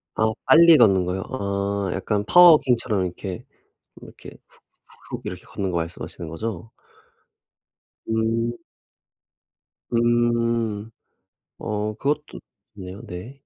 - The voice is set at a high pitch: No, low, 110 Hz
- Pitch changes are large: No, average, 3.5 semitones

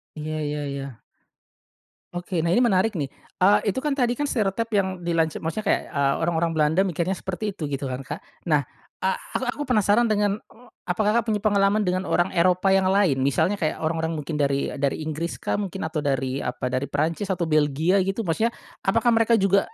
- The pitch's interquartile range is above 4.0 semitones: Yes, average, 5.0 semitones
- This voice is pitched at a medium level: Yes, medium, 180 Hz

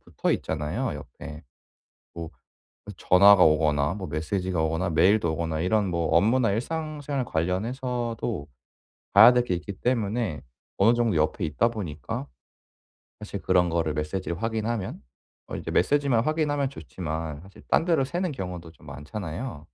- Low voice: Yes, very low, 95 Hz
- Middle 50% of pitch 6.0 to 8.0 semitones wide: Yes, wide, 6.6 semitones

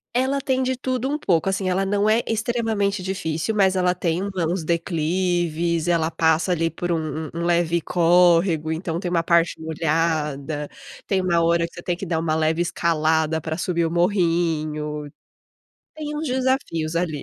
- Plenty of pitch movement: No, average, 3.0 semitones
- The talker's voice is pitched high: No, medium, 170 Hz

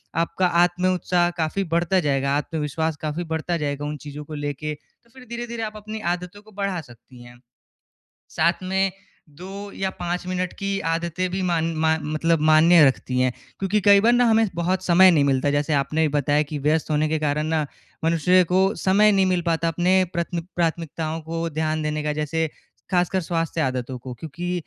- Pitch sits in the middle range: Yes, medium, 165 Hz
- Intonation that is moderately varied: Yes, average, 3.4 semitones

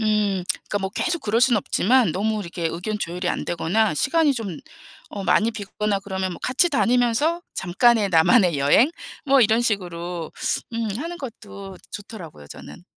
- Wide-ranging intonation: No, average, 4.8 semitones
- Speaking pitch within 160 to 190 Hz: No, high, 210 Hz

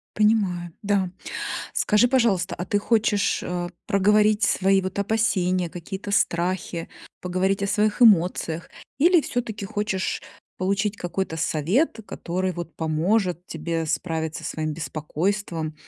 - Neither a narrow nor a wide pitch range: Yes, average, 3.4 semitones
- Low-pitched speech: No, high, 190 Hz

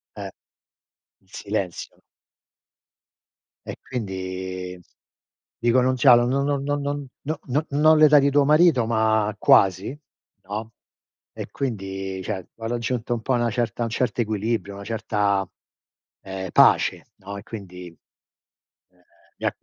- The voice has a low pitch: Yes, low, 115 Hz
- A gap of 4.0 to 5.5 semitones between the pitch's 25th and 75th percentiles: Yes, average, 5.0 semitones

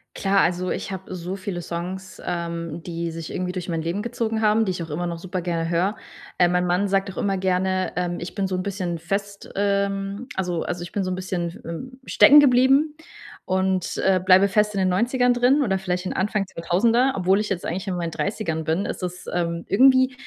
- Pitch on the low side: No, medium, 185 Hz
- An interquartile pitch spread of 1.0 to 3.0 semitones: Yes, narrow, 2.6 semitones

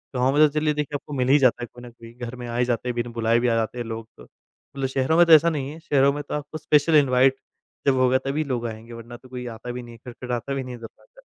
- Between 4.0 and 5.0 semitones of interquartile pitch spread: No, average, 3.2 semitones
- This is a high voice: No, low, 125 Hz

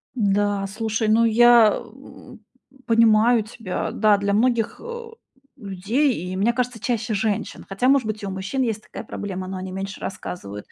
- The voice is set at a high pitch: Yes, high, 215 Hz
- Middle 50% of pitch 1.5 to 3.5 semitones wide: Yes, average, 3.2 semitones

